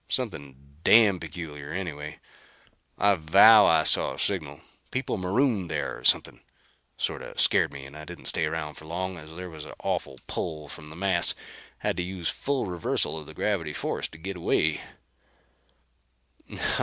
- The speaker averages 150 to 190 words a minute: Yes, average, 165 wpm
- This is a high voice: No, very low, 80 Hz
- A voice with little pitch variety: No, average, 3.5 semitones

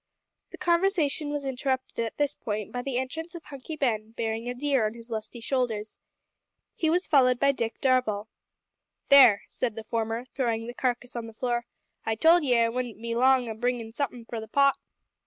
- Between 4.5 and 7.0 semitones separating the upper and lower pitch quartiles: No, average, 3.5 semitones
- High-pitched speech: Yes, high, 245 Hz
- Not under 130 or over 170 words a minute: No, average, 195 wpm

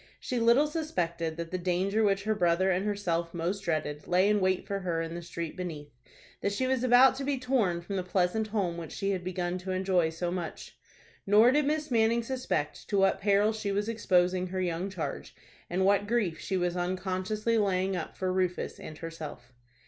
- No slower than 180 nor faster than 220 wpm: Yes, average, 200 wpm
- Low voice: No, medium, 185 Hz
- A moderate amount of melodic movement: Yes, average, 3.4 semitones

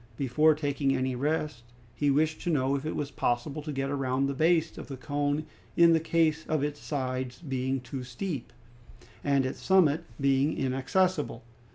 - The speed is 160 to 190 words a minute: Yes, average, 175 wpm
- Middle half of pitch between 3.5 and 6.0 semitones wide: No, average, 2.8 semitones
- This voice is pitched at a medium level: Yes, medium, 145 Hz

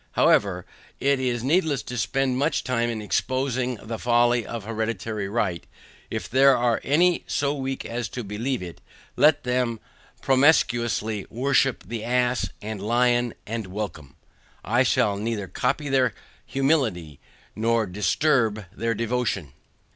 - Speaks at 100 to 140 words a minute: Yes, slow, 135 wpm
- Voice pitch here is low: Yes, low, 120 Hz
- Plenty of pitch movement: No, average, 3.4 semitones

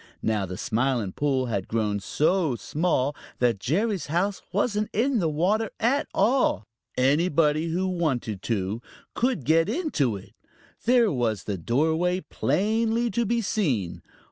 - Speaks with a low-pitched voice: No, medium, 160 Hz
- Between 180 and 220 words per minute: No, average, 140 wpm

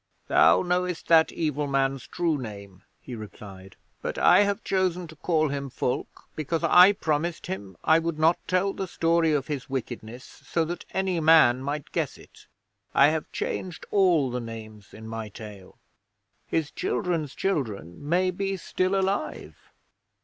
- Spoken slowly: No, average, 155 wpm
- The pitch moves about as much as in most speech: No, wide, 6.2 semitones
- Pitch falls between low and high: Yes, medium, 155 Hz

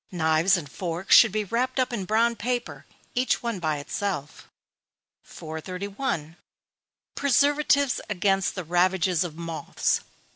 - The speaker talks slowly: Yes, slow, 120 wpm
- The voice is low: No, high, 195 Hz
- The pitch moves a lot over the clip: Yes, wide, 5.9 semitones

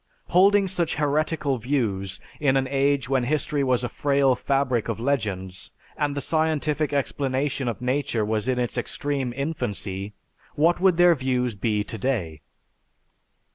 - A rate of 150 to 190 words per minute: No, slow, 135 wpm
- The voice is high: No, low, 135 Hz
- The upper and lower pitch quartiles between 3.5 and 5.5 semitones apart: Yes, average, 3.8 semitones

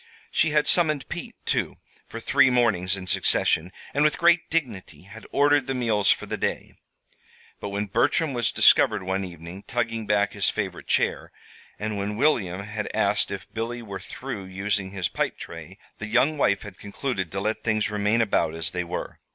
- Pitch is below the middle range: Yes, low, 105 Hz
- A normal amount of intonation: Yes, average, 4.4 semitones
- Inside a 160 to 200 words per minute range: Yes, average, 185 wpm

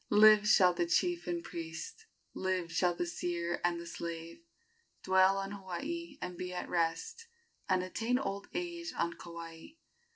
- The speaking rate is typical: Yes, average, 155 wpm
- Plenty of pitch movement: No, average, 4.1 semitones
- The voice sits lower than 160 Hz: No, medium, 185 Hz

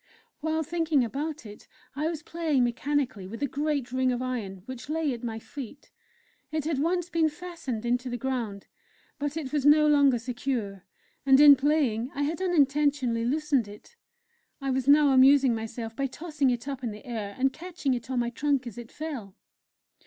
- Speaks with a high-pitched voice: Yes, very high, 270 Hz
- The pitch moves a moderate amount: Yes, average, 3.8 semitones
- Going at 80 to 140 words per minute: No, average, 185 wpm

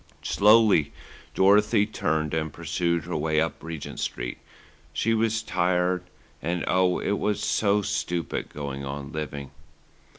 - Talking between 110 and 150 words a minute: Yes, slow, 135 wpm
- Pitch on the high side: No, very low, 85 Hz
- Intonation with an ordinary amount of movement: Yes, average, 4.8 semitones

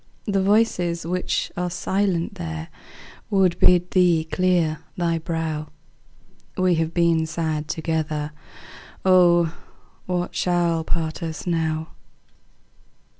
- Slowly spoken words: Yes, slow, 105 wpm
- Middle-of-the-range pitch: Yes, medium, 170 Hz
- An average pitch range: No, narrow, 2.1 semitones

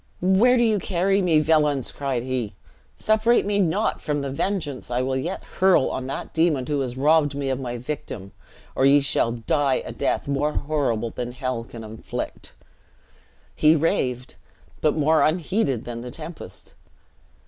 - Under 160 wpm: No, average, 165 wpm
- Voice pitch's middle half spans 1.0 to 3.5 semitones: No, average, 4.3 semitones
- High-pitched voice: No, medium, 145 Hz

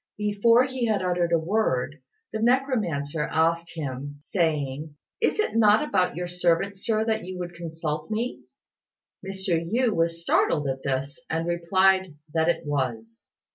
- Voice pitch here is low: No, medium, 170 Hz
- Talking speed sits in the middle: Yes, average, 150 wpm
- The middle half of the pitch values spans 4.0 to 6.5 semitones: Yes, average, 5.2 semitones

